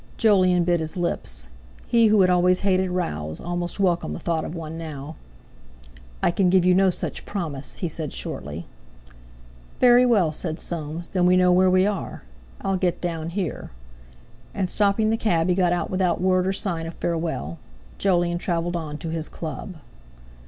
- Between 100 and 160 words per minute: No, average, 175 wpm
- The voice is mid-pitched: Yes, medium, 175 Hz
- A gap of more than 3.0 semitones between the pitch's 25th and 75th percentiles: No, narrow, 2.4 semitones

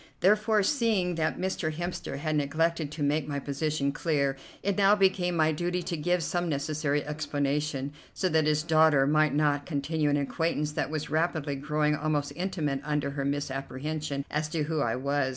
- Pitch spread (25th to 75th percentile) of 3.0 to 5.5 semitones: No, narrow, 2.6 semitones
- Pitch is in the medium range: Yes, medium, 150 Hz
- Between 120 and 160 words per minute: No, average, 175 wpm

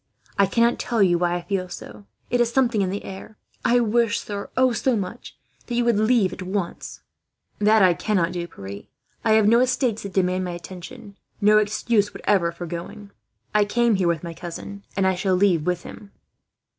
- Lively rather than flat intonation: No, average, 3.8 semitones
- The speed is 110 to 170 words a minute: No, average, 195 wpm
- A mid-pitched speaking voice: No, high, 200 Hz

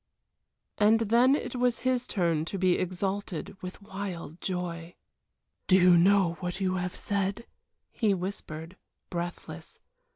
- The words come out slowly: Yes, slow, 130 wpm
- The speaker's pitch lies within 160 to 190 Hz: Yes, medium, 185 Hz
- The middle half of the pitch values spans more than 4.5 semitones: No, narrow, 2.5 semitones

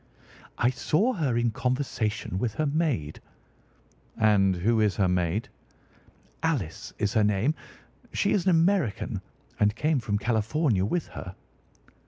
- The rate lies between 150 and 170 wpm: No, slow, 135 wpm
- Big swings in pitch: Yes, wide, 6.7 semitones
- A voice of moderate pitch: No, low, 115 Hz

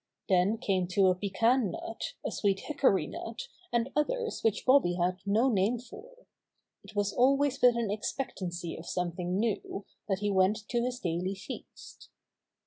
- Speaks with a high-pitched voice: Yes, high, 210 Hz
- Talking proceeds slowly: No, average, 160 wpm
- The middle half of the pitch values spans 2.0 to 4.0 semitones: No, average, 5.1 semitones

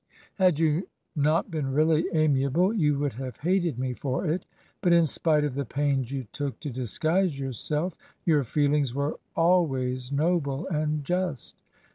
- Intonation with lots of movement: No, average, 3.5 semitones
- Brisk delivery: No, average, 155 wpm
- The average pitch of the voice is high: No, medium, 150 Hz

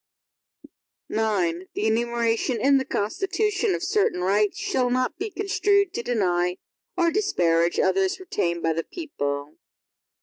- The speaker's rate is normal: No, slow, 130 wpm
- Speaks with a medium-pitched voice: No, high, 230 Hz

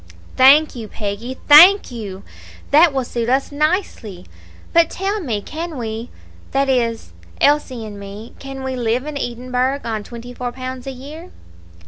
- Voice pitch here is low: No, very high, 255 Hz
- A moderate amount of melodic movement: Yes, average, 4.0 semitones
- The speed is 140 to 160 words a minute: Yes, average, 155 wpm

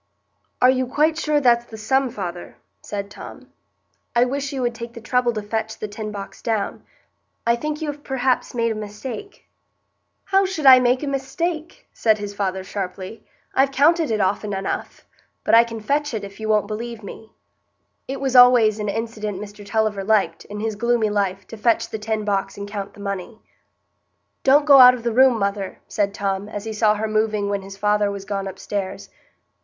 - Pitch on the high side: Yes, high, 220 Hz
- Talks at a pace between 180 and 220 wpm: Yes, average, 195 wpm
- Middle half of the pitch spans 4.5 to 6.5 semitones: No, average, 3.8 semitones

